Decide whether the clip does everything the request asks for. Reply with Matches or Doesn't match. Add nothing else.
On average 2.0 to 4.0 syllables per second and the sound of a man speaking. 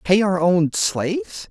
Matches